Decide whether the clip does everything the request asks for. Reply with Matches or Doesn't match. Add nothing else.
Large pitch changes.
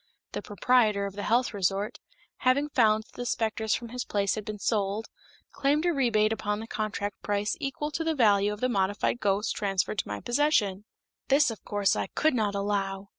Doesn't match